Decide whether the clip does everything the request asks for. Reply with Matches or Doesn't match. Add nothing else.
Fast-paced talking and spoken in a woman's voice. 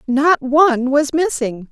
Doesn't match